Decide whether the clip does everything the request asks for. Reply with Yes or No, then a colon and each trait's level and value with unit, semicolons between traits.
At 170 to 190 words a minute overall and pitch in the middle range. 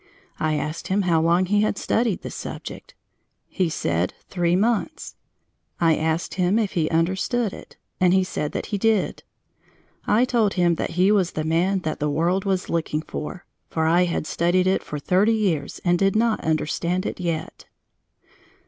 Yes: average, 175 wpm; medium, 180 Hz